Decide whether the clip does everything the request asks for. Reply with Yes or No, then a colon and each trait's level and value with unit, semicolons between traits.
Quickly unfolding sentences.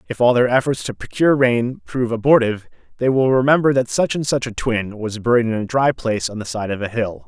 Yes: fast, 245 wpm